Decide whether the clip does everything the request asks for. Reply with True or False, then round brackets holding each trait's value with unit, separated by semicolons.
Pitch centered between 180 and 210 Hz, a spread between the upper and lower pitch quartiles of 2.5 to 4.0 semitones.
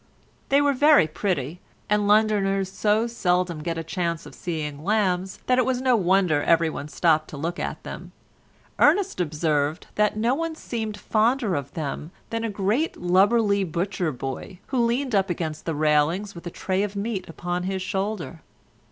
False (190 Hz; 4.8 semitones)